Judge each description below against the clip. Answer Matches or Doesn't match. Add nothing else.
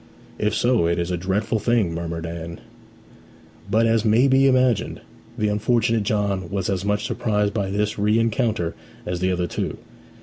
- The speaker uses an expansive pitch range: Doesn't match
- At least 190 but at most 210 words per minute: Doesn't match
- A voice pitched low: Matches